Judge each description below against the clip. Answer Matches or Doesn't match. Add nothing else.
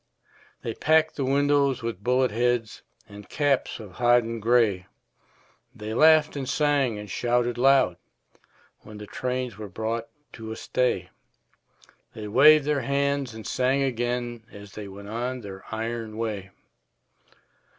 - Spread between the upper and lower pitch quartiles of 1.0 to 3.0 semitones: Doesn't match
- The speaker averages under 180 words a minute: Matches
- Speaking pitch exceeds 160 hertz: Doesn't match